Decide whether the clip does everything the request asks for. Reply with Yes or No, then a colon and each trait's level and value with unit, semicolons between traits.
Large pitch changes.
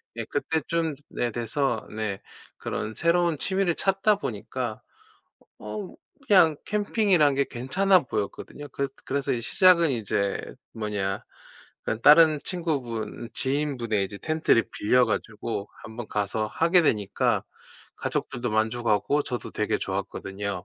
Yes: wide, 7.0 semitones